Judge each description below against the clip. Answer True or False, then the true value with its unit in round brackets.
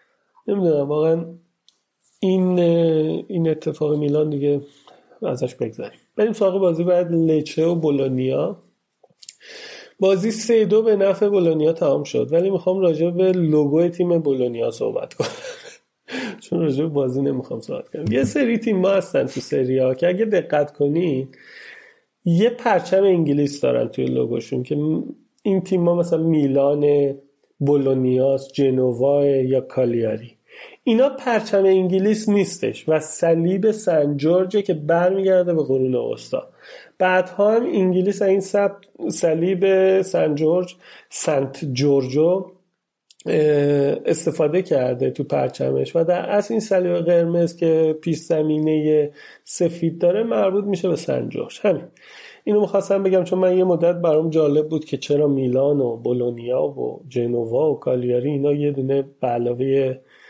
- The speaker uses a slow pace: False (135 wpm)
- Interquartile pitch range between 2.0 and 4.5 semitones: False (5.0 semitones)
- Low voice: False (170 Hz)